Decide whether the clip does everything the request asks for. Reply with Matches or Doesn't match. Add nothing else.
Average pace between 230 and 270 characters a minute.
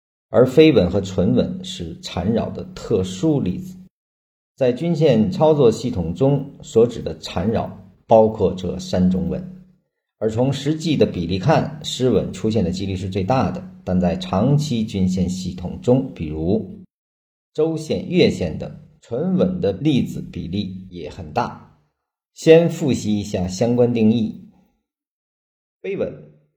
Doesn't match